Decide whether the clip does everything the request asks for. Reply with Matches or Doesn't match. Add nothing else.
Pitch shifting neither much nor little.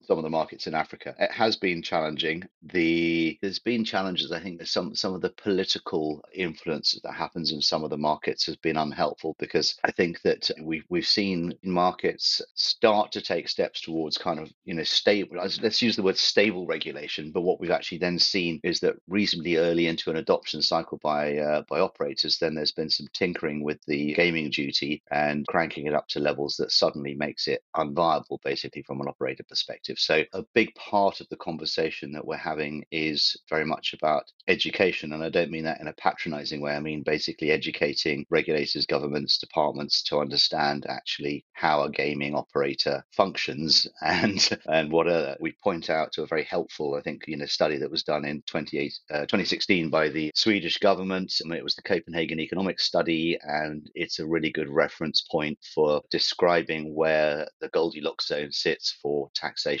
Doesn't match